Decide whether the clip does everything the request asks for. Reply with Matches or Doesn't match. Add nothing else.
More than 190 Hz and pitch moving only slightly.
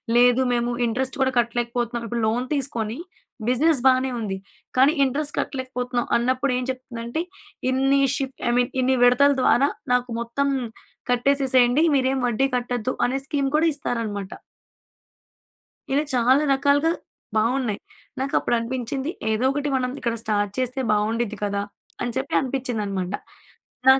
Matches